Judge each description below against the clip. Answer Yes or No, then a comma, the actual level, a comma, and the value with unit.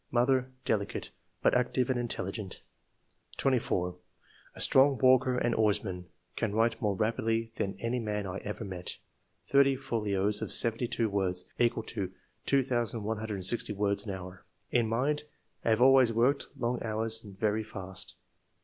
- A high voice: No, low, 110 Hz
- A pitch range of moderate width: Yes, average, 3.5 semitones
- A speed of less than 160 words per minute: Yes, average, 150 wpm